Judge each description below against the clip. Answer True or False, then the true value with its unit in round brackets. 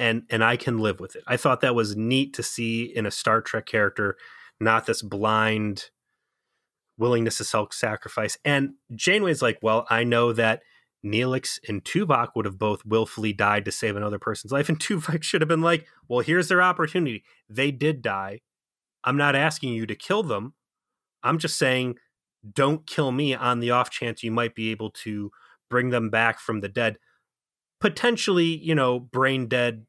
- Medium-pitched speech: False (120 Hz)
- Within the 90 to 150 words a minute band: False (185 wpm)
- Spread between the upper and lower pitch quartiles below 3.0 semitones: False (4.0 semitones)